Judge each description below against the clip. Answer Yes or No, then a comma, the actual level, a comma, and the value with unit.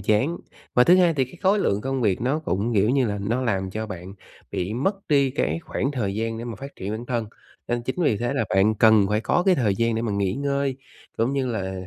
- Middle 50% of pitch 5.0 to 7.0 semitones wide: No, average, 4.5 semitones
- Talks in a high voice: No, low, 115 Hz